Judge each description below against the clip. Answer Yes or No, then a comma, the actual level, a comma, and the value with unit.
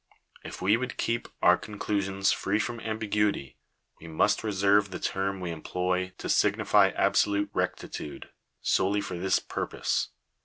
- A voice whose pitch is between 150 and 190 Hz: No, low, 100 Hz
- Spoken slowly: No, average, 155 wpm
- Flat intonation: Yes, narrow, 2.2 semitones